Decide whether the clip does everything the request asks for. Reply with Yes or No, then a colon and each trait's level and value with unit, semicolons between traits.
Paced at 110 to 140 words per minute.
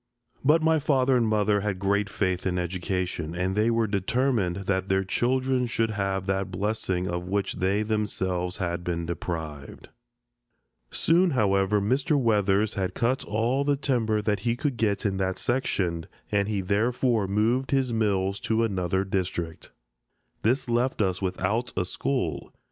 No: average, 155 wpm